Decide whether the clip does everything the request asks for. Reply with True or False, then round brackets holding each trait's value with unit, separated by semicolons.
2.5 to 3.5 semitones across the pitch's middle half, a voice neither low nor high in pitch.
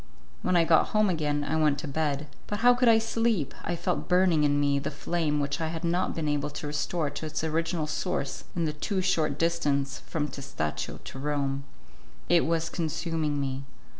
True (2.8 semitones; 155 Hz)